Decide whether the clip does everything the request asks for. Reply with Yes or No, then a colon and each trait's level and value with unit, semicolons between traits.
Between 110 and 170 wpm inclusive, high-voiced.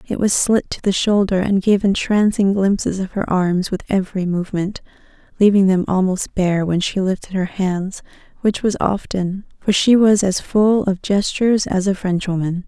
No: average, 180 wpm; high, 195 Hz